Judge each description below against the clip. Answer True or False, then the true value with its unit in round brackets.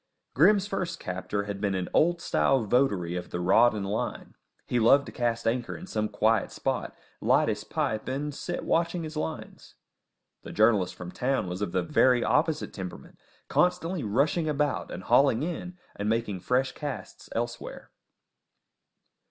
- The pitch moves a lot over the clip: True (6.7 semitones)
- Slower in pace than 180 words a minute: True (160 wpm)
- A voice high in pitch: False (120 Hz)